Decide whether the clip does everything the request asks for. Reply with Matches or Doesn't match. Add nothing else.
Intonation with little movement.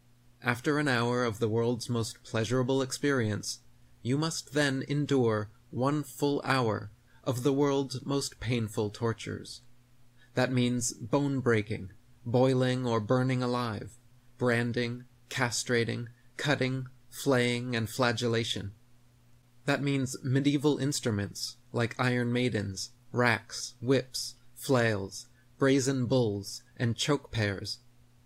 Matches